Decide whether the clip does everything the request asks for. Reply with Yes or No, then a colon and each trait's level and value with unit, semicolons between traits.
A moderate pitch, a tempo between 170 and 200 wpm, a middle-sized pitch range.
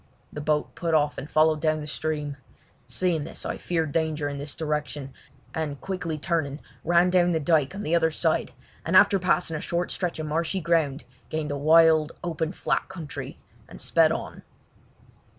No: medium, 160 Hz; average, 180 wpm; narrow, 2.2 semitones